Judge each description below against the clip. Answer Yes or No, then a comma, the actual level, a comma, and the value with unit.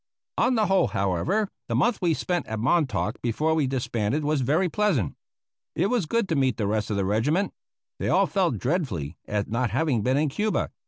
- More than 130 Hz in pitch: Yes, medium, 140 Hz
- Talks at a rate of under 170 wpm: No, average, 200 wpm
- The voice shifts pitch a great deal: Yes, wide, 8.3 semitones